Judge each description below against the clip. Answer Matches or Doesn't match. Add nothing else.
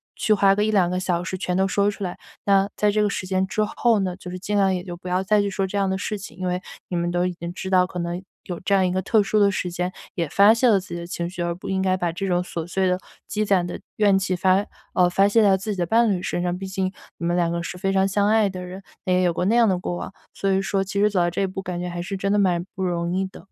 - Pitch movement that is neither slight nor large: Doesn't match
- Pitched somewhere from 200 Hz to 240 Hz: Doesn't match